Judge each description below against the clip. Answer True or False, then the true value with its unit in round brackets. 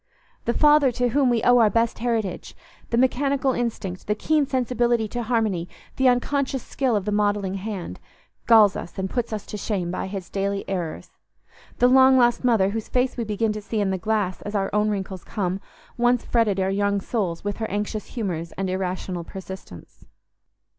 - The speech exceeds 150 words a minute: True (180 wpm)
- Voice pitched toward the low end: False (215 Hz)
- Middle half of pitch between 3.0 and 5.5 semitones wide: True (4.0 semitones)